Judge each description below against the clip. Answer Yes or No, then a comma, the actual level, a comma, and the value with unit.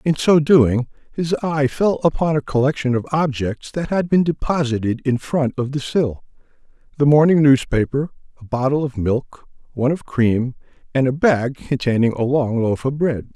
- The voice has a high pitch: No, low, 135 Hz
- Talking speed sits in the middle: Yes, average, 170 wpm